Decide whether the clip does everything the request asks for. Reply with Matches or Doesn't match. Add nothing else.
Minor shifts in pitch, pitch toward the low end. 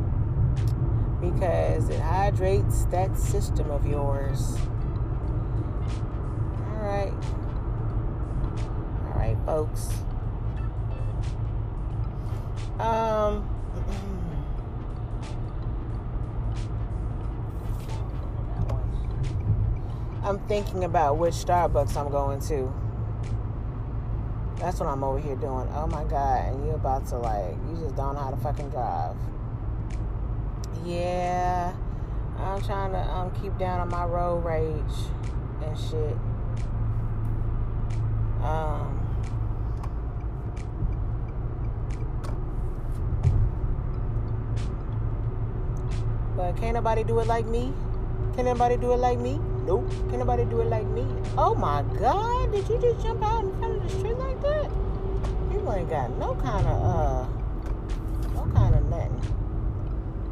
Matches